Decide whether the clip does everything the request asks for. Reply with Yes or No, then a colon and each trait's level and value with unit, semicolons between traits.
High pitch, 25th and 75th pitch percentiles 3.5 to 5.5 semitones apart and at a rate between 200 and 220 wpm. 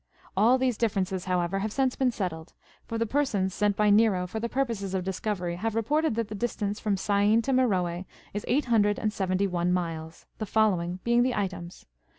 Yes: high, 205 Hz; average, 3.8 semitones; fast, 205 wpm